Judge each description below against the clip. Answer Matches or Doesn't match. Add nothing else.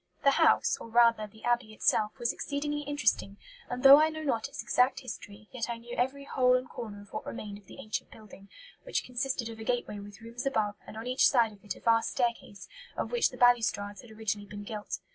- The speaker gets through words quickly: Matches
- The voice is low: Doesn't match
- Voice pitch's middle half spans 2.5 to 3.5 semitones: Matches